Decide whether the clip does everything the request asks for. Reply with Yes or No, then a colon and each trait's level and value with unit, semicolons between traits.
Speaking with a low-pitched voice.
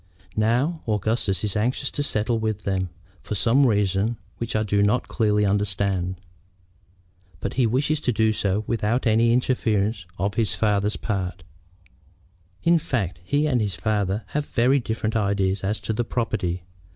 Yes: low, 110 Hz